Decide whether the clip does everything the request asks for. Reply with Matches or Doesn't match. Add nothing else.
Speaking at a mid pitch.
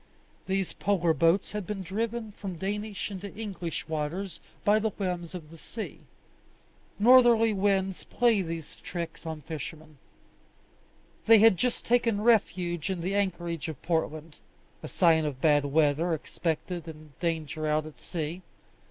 Matches